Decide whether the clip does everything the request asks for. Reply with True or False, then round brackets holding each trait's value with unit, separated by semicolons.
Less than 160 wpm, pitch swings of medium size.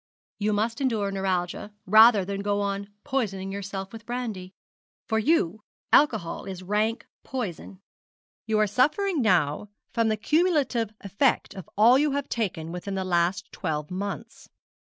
True (145 wpm; 3.5 semitones)